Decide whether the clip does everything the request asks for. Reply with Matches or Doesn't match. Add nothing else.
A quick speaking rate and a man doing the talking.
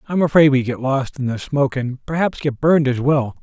Matches